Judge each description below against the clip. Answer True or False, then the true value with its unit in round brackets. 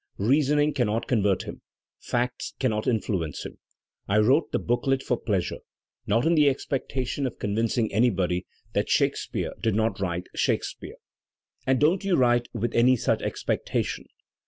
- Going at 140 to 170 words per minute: True (155 wpm)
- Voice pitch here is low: True (120 Hz)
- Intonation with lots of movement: False (3.9 semitones)